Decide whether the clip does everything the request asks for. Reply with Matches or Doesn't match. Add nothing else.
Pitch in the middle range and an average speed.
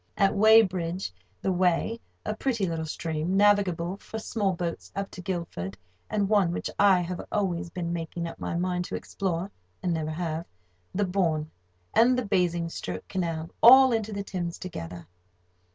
Matches